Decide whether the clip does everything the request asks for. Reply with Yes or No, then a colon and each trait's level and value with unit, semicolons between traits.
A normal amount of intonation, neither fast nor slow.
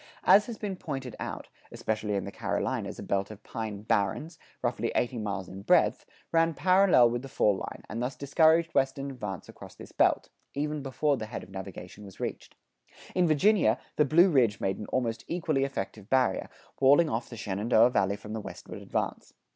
No: wide, 6.3 semitones; average, 185 wpm